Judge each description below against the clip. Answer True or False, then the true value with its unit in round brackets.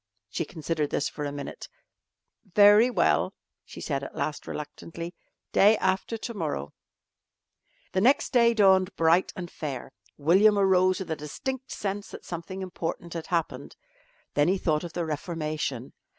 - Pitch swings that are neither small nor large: True (4.3 semitones)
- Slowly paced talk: False (150 wpm)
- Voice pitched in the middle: True (175 Hz)